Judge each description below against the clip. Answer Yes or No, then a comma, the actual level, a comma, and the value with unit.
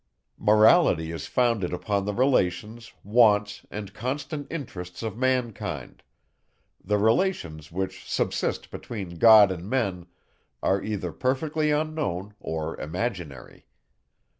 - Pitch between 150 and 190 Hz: No, low, 105 Hz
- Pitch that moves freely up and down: Yes, wide, 5.9 semitones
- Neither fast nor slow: No, slow, 110 wpm